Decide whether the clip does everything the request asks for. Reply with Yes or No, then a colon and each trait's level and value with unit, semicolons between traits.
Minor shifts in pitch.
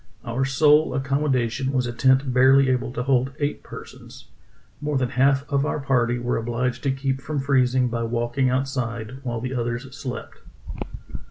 Yes: narrow, 2.0 semitones